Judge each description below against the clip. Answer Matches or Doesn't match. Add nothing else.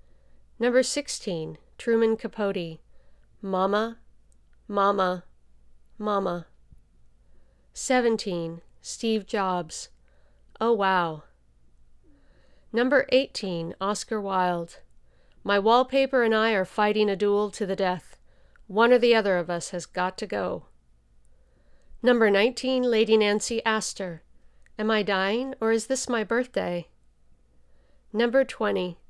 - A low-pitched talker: Doesn't match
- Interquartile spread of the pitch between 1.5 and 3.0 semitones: Doesn't match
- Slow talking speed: Matches